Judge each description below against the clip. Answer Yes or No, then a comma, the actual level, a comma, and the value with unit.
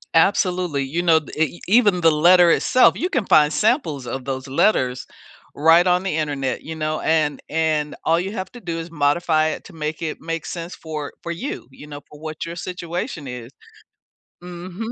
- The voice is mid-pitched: Yes, medium, 165 Hz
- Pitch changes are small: No, average, 3.0 semitones